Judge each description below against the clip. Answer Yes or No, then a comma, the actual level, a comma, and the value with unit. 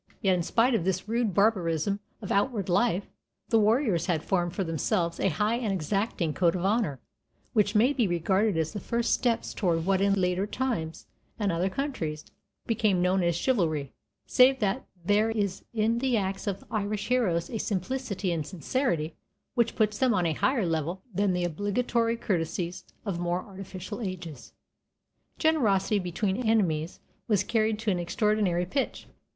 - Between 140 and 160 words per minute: No, average, 170 wpm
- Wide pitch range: No, average, 4.2 semitones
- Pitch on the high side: Yes, high, 195 Hz